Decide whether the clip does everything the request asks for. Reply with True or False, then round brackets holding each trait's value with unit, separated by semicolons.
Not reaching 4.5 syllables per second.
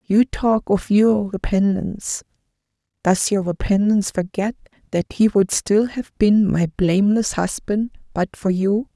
True (4.2 syllables/s)